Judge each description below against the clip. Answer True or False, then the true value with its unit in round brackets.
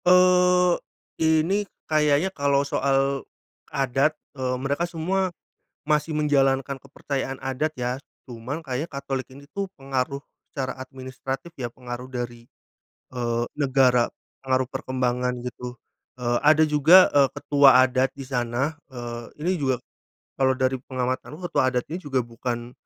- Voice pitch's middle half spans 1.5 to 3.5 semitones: True (2.9 semitones)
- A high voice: False (135 Hz)